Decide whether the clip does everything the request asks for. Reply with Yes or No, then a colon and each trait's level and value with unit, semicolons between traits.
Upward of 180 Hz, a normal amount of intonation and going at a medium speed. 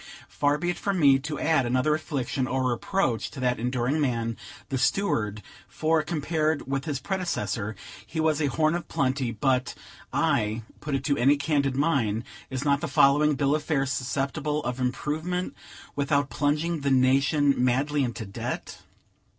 No: medium, 140 Hz; average, 3.1 semitones; average, 165 wpm